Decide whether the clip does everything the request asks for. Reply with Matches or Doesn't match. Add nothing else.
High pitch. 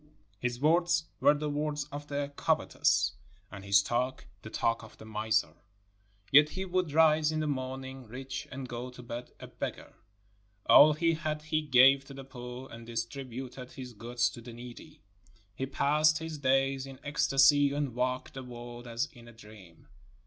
Doesn't match